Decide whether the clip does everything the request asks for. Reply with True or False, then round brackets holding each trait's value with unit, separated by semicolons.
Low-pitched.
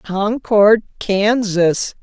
False (205 Hz)